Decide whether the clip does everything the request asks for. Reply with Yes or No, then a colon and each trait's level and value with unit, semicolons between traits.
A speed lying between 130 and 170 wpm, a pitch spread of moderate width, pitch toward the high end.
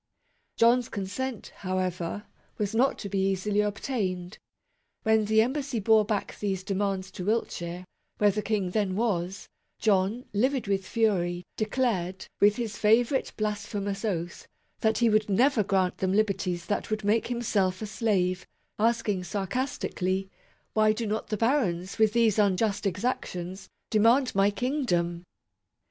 Yes: average, 145 wpm; average, 3.0 semitones; high, 205 Hz